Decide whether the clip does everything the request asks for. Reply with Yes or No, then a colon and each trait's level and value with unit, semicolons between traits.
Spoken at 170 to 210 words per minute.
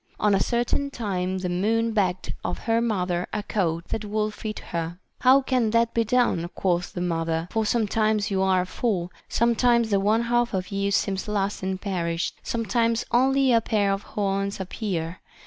Yes: average, 180 wpm